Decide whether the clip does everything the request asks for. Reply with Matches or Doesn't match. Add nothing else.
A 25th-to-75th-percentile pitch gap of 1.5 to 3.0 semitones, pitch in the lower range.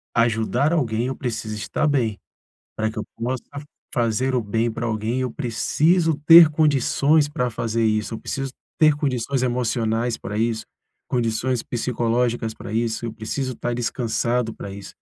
Matches